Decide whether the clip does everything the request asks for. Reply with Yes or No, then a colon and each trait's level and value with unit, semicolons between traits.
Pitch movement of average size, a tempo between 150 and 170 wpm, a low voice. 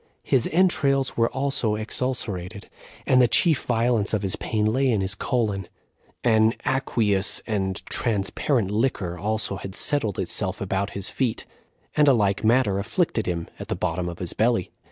Yes: average, 4.4 semitones; average, 165 wpm; low, 110 Hz